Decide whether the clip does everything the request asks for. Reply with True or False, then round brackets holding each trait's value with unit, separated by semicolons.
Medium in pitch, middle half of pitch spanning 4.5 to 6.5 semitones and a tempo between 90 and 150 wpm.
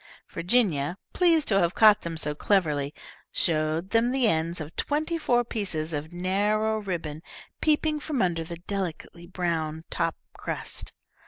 True (180 Hz; 5.4 semitones; 145 wpm)